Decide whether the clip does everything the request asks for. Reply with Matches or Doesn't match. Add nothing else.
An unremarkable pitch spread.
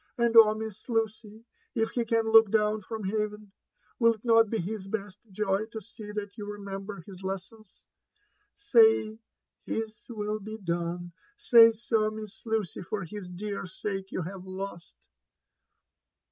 Doesn't match